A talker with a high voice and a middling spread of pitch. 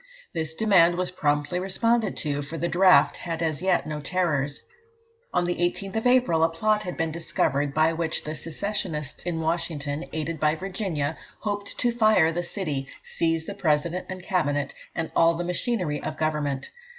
No: medium, 165 Hz; average, 3.4 semitones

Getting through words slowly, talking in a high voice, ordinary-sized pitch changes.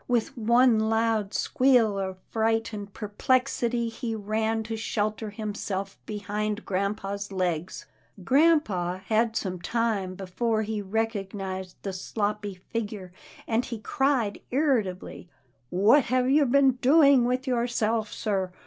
Yes: slow, 125 wpm; high, 220 Hz; average, 3.2 semitones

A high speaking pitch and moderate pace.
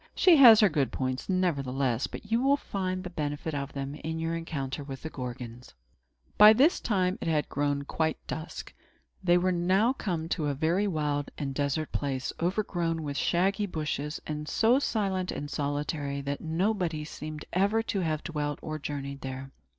No: medium, 155 Hz; average, 175 wpm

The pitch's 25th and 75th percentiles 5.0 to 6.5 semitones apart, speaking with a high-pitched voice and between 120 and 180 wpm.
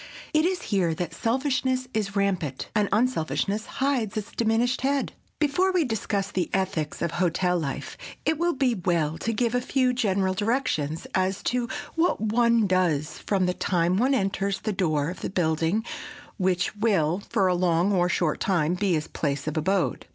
Yes: average, 5.3 semitones; high, 195 Hz; average, 175 wpm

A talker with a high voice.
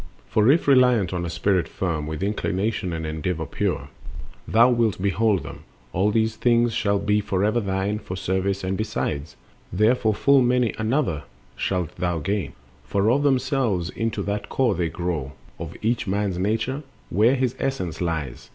No: low, 100 Hz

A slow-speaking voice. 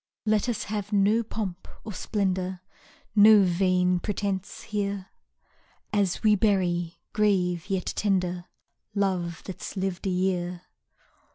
Yes: slow, 115 wpm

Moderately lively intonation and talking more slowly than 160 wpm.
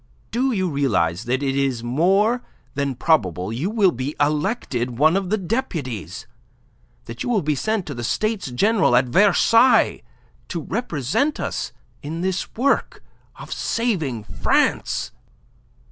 No: wide, 8.8 semitones; average, 140 wpm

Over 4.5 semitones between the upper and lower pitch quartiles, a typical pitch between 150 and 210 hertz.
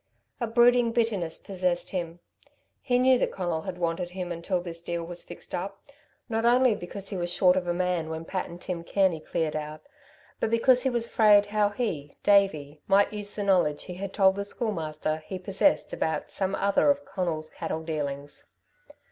No: average, 3.7 semitones; medium, 185 Hz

